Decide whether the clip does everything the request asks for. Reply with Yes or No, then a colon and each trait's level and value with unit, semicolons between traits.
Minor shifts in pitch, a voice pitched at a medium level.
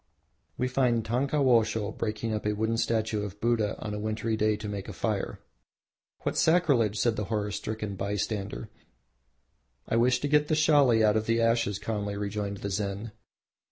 No: narrow, 2.2 semitones; low, 110 Hz